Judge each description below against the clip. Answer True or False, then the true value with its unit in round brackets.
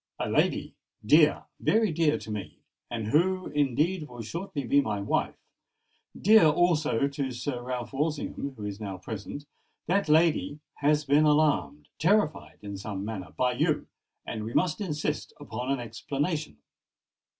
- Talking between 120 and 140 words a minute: True (135 wpm)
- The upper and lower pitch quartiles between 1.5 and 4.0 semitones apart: False (5.6 semitones)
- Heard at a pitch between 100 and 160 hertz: True (140 Hz)